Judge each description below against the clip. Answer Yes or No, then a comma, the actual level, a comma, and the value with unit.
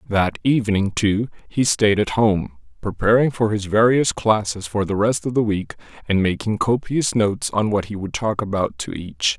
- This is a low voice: Yes, low, 110 Hz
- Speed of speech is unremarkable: Yes, average, 190 wpm